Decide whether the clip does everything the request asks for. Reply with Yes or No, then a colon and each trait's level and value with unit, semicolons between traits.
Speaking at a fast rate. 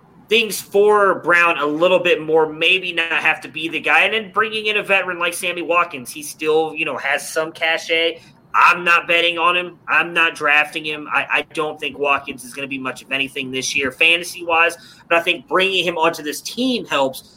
Yes: fast, 220 wpm